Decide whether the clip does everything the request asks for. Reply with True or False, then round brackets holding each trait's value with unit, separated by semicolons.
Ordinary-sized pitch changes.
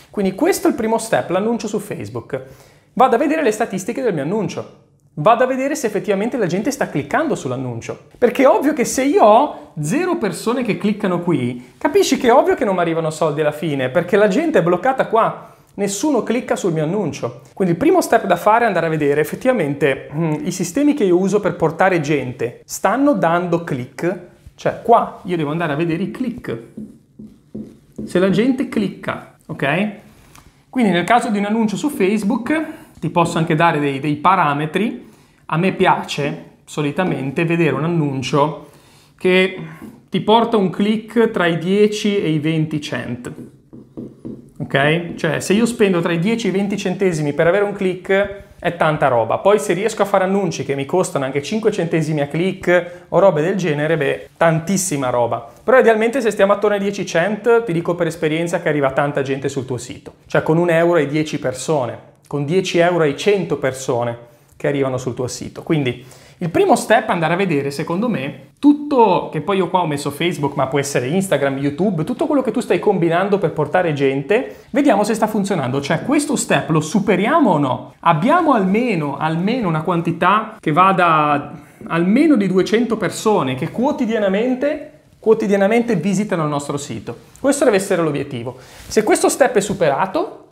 False (6.1 semitones)